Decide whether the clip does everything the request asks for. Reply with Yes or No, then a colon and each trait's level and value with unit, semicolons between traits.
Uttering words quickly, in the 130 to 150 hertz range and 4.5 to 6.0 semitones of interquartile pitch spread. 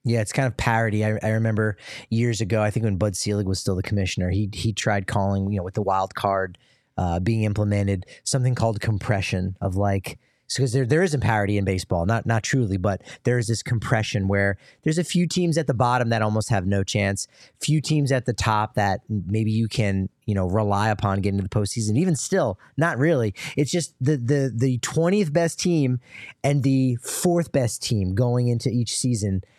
No: fast, 215 wpm; low, 110 Hz; average, 4.8 semitones